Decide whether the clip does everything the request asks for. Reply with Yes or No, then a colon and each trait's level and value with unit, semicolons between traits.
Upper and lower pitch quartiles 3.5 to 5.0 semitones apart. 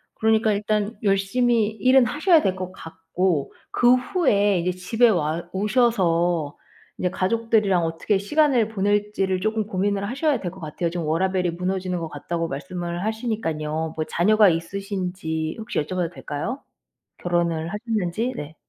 Yes: average, 4.2 semitones